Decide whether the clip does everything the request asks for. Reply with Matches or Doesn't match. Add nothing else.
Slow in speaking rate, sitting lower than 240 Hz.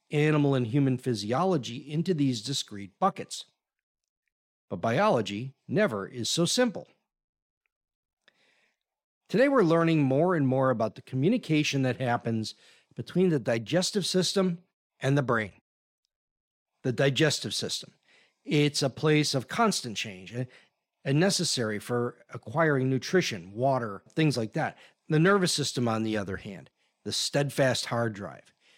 Matches